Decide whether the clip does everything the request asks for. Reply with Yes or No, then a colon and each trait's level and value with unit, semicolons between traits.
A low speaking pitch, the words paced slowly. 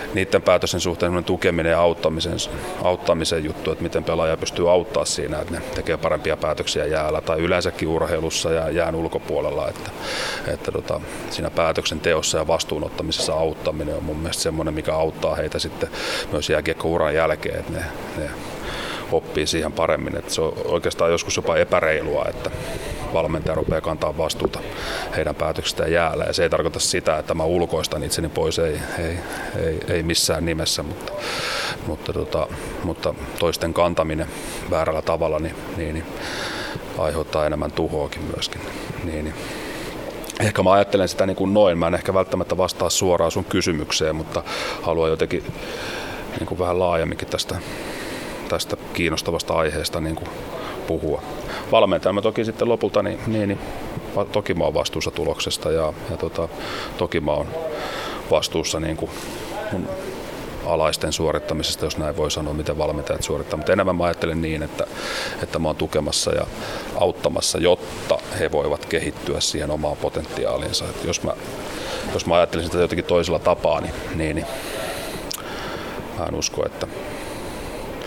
No: very low, 90 Hz; average, 150 wpm